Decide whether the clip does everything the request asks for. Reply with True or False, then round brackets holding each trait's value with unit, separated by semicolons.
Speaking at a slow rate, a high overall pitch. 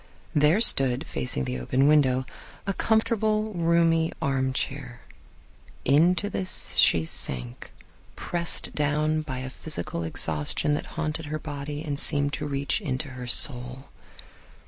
False (125 wpm; 145 Hz)